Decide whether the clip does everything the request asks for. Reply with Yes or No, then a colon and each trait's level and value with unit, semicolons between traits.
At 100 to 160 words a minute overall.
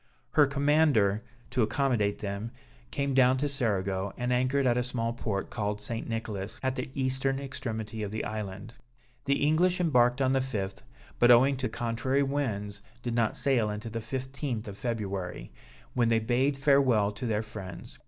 No: average, 170 wpm